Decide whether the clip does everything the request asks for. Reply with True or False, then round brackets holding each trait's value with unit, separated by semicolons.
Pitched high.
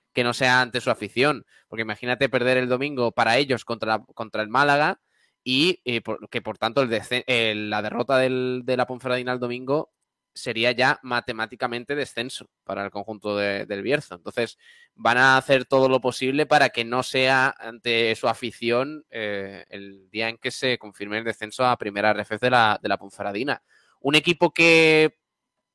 False (125 Hz)